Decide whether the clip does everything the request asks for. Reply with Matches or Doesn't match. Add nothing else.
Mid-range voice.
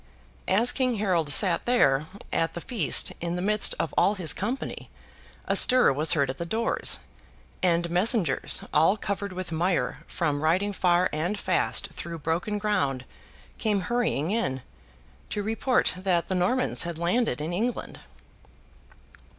Matches